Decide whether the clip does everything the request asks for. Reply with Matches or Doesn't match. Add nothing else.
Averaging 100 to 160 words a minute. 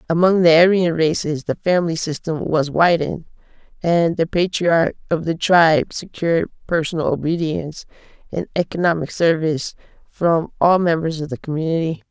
Matches